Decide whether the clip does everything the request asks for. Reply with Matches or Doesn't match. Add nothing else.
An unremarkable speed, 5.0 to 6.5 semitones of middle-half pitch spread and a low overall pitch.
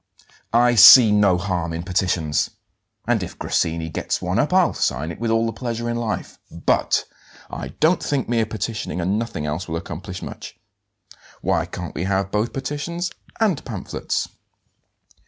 Matches